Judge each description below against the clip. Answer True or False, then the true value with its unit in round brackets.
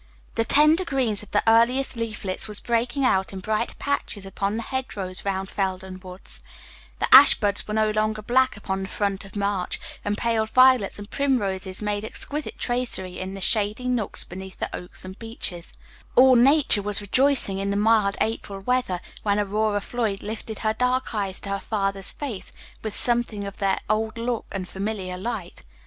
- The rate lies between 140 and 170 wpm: False (180 wpm)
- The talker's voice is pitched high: True (210 Hz)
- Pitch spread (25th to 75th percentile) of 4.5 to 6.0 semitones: False (3.3 semitones)